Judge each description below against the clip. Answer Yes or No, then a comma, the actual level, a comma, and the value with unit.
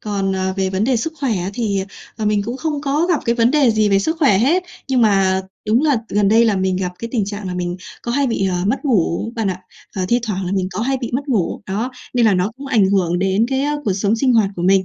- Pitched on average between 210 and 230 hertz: Yes, high, 215 Hz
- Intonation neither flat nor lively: Yes, average, 4.7 semitones